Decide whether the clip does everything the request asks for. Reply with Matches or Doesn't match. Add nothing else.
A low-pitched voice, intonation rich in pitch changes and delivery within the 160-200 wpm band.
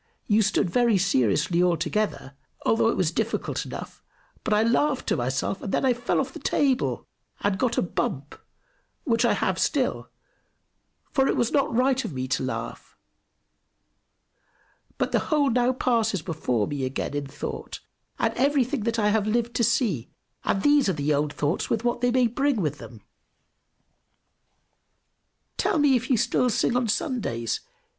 Doesn't match